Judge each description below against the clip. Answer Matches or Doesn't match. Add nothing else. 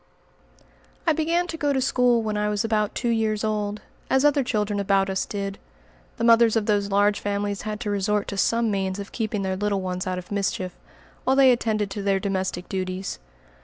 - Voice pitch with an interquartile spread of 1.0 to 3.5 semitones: Matches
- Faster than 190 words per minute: Matches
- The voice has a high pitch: Matches